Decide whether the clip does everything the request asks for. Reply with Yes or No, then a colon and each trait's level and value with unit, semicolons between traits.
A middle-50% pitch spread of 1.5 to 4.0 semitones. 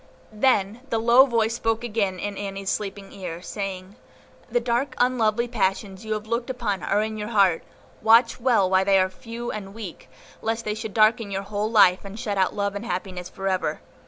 Yes: average, 2.9 semitones